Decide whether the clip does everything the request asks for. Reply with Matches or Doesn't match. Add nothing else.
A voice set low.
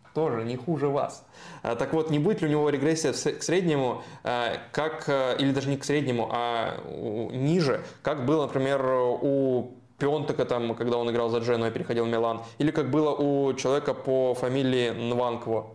Matches